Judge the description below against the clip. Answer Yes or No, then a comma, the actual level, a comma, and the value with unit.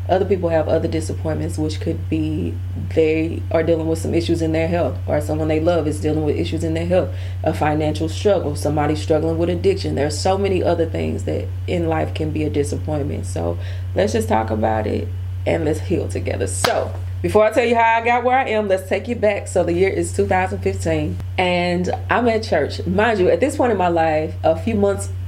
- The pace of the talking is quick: Yes, fast, 220 wpm